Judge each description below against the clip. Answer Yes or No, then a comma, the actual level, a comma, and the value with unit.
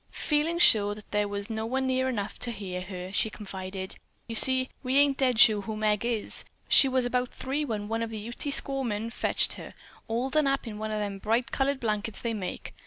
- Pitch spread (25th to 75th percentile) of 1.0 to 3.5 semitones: No, average, 3.9 semitones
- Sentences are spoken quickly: Yes, fast, 225 wpm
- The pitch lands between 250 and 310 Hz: No, high, 225 Hz